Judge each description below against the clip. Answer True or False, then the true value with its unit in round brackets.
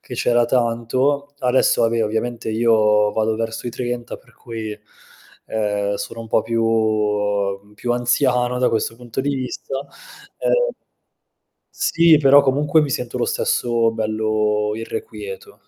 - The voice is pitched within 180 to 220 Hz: False (115 Hz)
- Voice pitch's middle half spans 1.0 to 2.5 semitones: False (2.9 semitones)